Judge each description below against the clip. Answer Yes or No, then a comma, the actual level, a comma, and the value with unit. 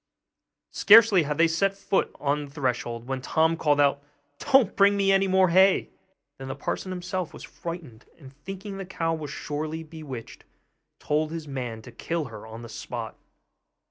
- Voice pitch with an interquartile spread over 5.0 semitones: Yes, wide, 5.4 semitones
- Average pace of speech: Yes, average, 175 wpm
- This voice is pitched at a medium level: Yes, medium, 160 Hz